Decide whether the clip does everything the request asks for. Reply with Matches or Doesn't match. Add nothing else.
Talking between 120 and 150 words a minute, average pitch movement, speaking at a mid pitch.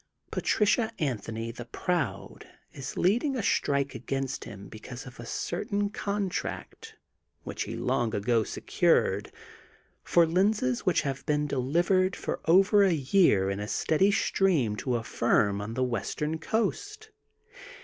Doesn't match